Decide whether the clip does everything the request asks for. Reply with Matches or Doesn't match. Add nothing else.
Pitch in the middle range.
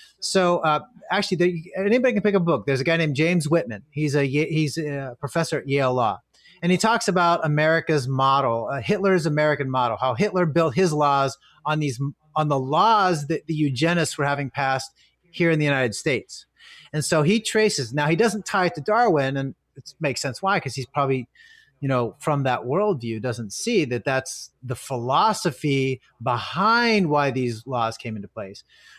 Matches